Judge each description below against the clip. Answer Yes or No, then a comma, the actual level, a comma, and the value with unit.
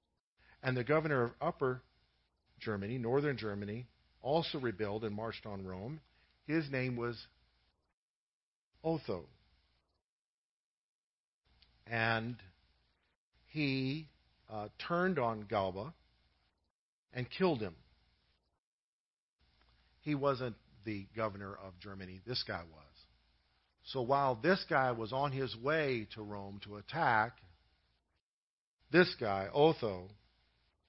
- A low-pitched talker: Yes, low, 105 Hz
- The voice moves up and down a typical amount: No, wide, 9.0 semitones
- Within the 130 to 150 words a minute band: No, slow, 100 wpm